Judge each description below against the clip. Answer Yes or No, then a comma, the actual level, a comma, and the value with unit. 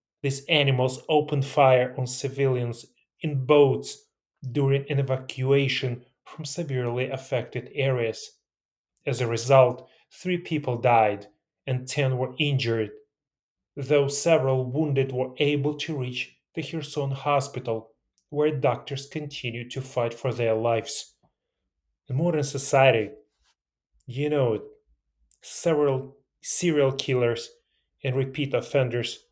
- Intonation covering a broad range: No, narrow, 2.5 semitones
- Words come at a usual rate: No, slow, 110 wpm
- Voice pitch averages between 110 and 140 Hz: Yes, low, 135 Hz